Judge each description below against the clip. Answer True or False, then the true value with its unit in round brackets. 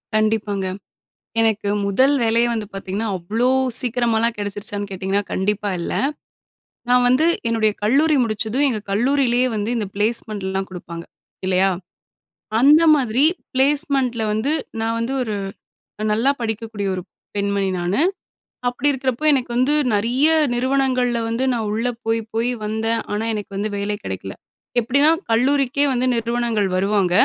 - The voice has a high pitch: True (225 Hz)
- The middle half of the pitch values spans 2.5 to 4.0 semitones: True (3.5 semitones)